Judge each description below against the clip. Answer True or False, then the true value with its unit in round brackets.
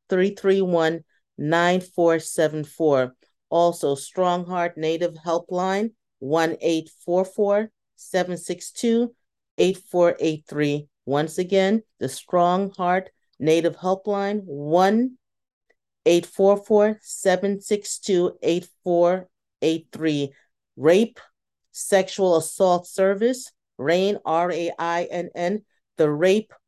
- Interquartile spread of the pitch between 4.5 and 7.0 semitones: False (3.1 semitones)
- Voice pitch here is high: False (175 Hz)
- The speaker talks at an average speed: False (65 wpm)